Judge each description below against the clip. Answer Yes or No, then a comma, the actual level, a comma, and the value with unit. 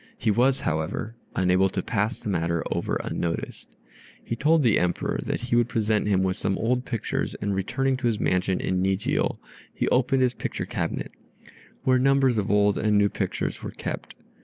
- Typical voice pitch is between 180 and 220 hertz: No, low, 105 Hz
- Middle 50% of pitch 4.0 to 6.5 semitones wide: Yes, average, 4.8 semitones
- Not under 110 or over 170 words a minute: No, average, 185 wpm